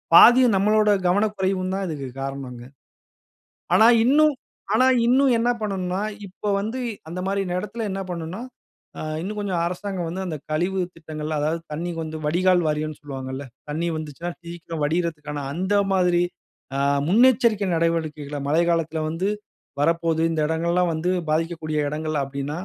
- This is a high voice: No, medium, 170 Hz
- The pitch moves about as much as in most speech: Yes, average, 3.7 semitones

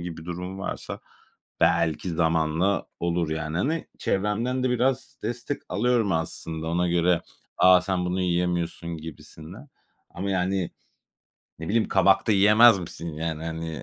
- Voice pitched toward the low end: Yes, very low, 90 Hz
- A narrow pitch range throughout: No, average, 3.5 semitones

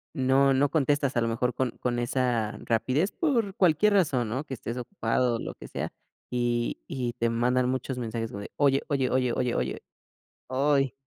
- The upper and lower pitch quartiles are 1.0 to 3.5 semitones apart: Yes, average, 2.8 semitones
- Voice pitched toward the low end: Yes, low, 130 Hz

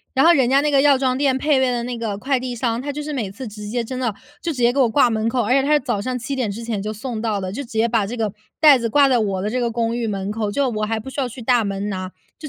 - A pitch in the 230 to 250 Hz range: Yes, high, 240 Hz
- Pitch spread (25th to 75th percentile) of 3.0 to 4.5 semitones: Yes, average, 3.5 semitones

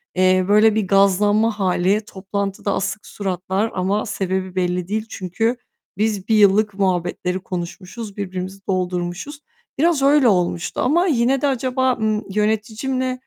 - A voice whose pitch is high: Yes, high, 205 Hz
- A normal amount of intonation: Yes, average, 3.2 semitones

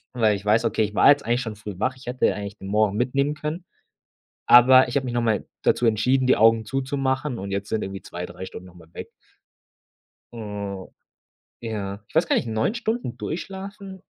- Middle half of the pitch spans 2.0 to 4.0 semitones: No, average, 4.5 semitones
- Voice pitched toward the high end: No, low, 115 Hz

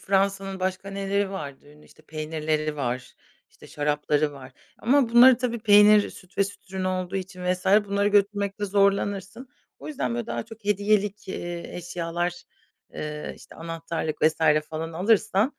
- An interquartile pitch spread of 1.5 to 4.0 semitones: No, average, 4.5 semitones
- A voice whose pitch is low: No, high, 190 Hz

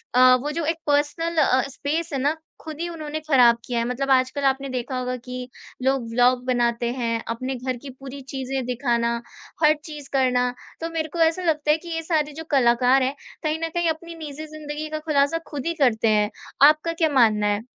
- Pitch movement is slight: No, average, 3.7 semitones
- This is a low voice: No, very high, 275 Hz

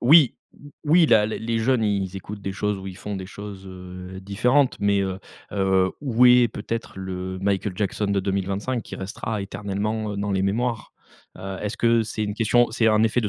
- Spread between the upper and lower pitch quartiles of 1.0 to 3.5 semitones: Yes, average, 2.7 semitones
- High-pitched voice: No, low, 105 Hz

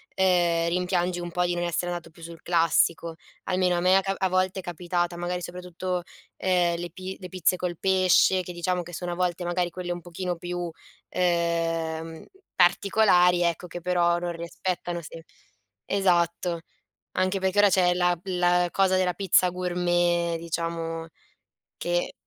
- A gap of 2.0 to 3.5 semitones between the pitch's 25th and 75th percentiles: No, narrow, 1.1 semitones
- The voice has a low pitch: No, medium, 175 Hz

